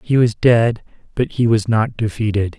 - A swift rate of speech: No, average, 185 wpm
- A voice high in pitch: No, low, 115 Hz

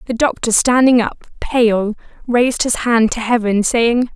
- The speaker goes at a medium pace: Yes, average, 160 wpm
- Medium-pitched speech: No, high, 235 Hz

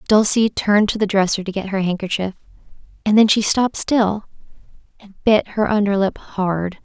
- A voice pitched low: No, high, 205 Hz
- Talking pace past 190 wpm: No, average, 165 wpm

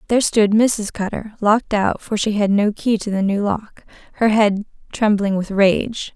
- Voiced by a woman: Yes, female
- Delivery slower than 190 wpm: Yes, average, 175 wpm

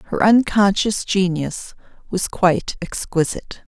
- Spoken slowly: Yes, slow, 95 wpm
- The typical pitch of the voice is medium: No, high, 195 Hz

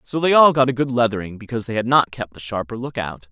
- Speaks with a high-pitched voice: No, low, 120 Hz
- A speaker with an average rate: No, fast, 290 wpm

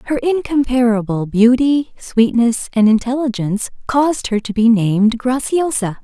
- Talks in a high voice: Yes, high, 240 Hz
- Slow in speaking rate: Yes, slow, 120 wpm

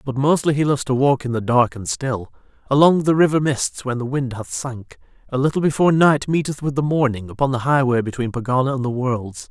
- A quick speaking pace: Yes, fast, 225 wpm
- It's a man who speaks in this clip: Yes, male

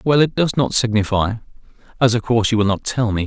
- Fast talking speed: Yes, fast, 240 wpm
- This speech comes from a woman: No, male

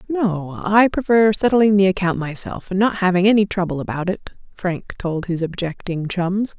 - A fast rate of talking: No, average, 175 wpm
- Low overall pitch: No, high, 190 Hz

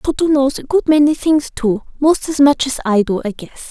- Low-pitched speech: No, very high, 275 Hz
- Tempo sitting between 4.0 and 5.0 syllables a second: No, 5.3 syllables/s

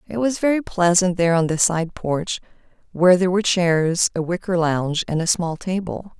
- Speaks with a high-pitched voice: No, medium, 180 Hz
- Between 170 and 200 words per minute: Yes, average, 195 wpm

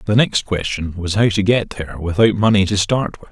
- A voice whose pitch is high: No, low, 100 Hz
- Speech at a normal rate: No, fast, 235 wpm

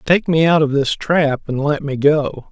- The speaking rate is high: Yes, fast, 240 wpm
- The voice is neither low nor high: Yes, medium, 150 Hz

